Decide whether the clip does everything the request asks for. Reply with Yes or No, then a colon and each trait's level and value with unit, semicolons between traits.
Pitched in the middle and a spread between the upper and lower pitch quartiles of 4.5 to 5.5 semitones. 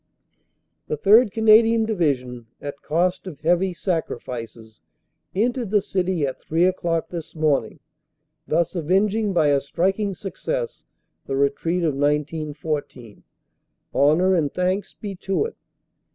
Yes: medium, 170 Hz; average, 5.1 semitones